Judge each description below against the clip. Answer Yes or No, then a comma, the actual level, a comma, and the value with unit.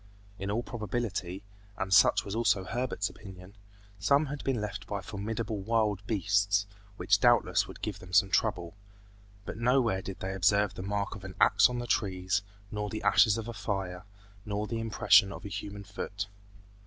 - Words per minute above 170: Yes, average, 180 wpm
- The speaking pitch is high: No, low, 100 Hz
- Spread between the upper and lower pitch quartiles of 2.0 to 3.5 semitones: Yes, narrow, 2.4 semitones